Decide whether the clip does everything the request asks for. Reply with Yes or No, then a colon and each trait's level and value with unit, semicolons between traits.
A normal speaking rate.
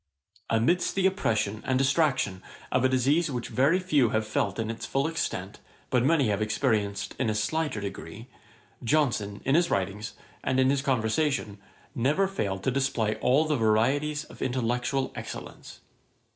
Yes: average, 160 wpm